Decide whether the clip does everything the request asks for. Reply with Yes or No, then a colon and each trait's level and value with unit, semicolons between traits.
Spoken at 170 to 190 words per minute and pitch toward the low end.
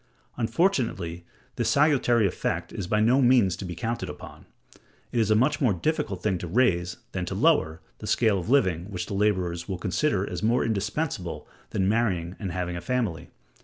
Yes: average, 185 wpm; low, 100 Hz